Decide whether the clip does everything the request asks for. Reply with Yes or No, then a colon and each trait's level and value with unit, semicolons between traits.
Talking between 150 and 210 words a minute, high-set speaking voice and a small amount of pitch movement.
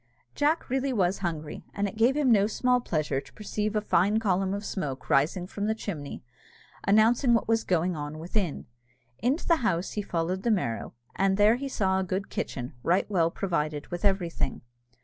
No: average, 190 wpm; high, 195 Hz; average, 4.5 semitones